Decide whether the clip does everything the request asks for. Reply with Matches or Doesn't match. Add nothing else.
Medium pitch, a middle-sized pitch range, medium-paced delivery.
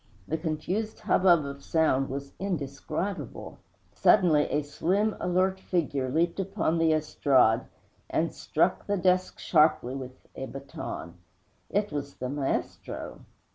Doesn't match